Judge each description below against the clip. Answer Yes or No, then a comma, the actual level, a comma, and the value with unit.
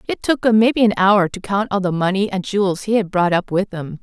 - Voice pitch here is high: Yes, high, 200 Hz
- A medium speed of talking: No, fast, 285 wpm